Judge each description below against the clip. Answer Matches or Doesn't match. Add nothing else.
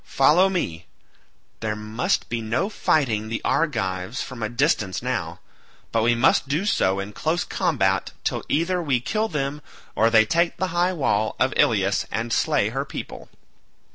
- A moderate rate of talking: Matches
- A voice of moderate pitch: Doesn't match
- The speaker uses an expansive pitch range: Matches